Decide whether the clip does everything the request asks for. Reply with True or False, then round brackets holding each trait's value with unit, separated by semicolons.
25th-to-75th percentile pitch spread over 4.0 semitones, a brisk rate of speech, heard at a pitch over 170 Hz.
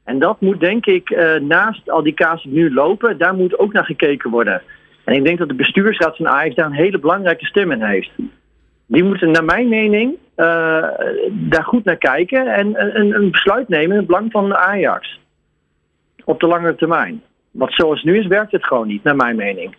True (5.1 semitones; 205 wpm; 185 Hz)